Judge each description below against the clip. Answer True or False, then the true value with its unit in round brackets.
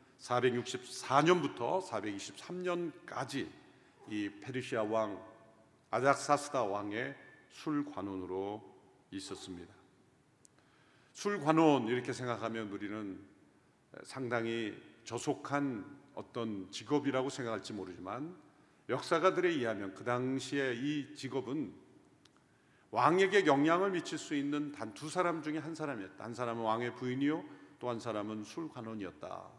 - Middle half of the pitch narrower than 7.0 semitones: True (5.2 semitones)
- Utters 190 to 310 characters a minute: True (250 characters per minute)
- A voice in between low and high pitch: False (125 Hz)